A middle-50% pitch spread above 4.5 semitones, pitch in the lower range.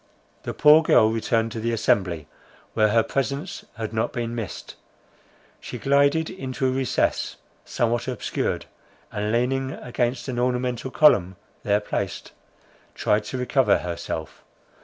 No: average, 3.4 semitones; low, 120 Hz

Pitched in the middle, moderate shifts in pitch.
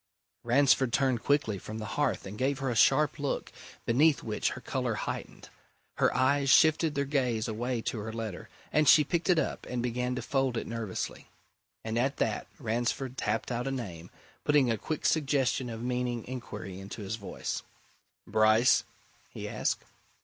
No: low, 125 Hz; average, 3.6 semitones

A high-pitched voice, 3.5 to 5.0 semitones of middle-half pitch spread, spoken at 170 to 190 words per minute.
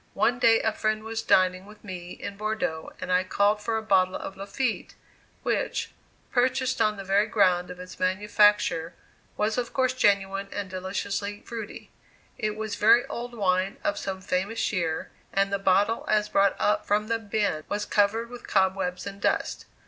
No: high, 205 Hz; narrow, 2.5 semitones; average, 175 wpm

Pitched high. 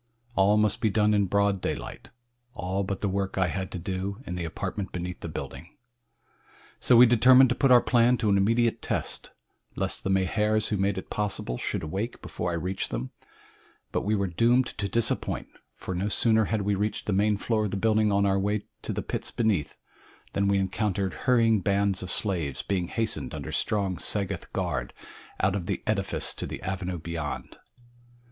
No: low, 100 Hz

